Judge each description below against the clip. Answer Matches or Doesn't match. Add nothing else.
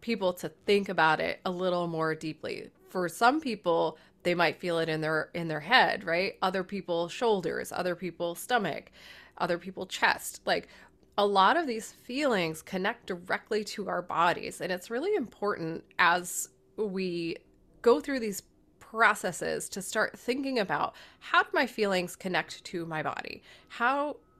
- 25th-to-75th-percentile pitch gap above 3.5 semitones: Matches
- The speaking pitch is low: Doesn't match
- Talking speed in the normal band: Matches